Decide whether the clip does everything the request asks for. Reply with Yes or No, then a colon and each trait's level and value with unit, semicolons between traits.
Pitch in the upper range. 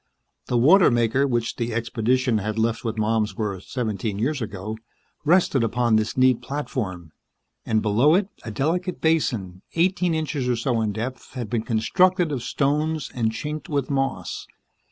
No: low, 120 Hz